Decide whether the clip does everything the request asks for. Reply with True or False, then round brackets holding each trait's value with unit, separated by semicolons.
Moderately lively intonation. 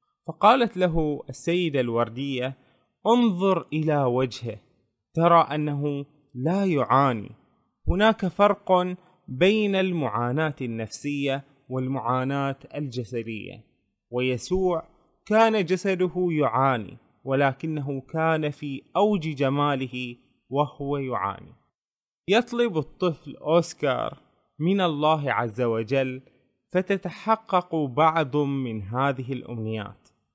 False (5.8 semitones)